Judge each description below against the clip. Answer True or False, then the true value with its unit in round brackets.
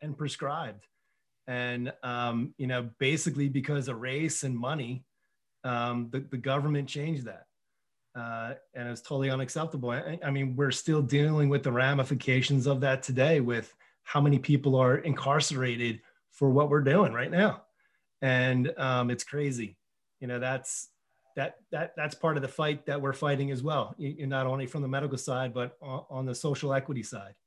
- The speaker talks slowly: False (175 wpm)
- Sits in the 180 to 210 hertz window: False (135 Hz)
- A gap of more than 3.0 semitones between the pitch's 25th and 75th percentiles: False (2.4 semitones)